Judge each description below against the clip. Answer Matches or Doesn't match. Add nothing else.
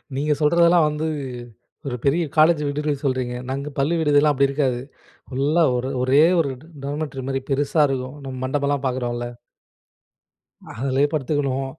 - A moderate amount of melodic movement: Doesn't match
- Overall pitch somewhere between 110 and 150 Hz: Matches